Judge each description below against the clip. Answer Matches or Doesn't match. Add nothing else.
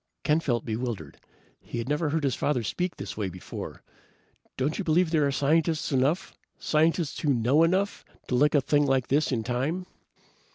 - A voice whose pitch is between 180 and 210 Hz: Doesn't match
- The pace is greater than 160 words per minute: Matches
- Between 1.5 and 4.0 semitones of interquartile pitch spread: Doesn't match